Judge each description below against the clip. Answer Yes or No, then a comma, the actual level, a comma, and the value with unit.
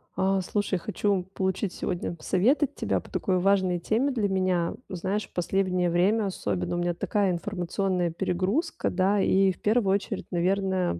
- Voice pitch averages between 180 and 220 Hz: Yes, high, 190 Hz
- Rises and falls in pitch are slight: Yes, narrow, 2.1 semitones